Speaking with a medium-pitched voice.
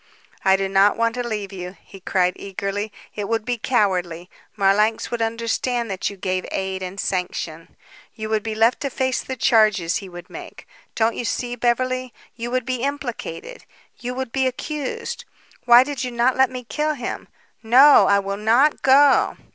No: high, 230 Hz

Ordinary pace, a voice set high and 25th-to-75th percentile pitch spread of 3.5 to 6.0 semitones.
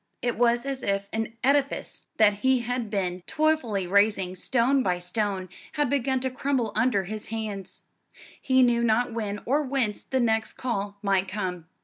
Yes: average, 165 wpm; high, 225 Hz; average, 4.3 semitones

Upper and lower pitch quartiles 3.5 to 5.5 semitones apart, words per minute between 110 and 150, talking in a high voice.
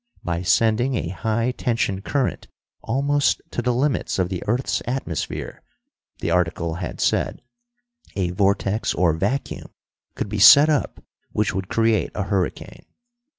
No: average, 5.2 semitones; average, 140 wpm; low, 105 Hz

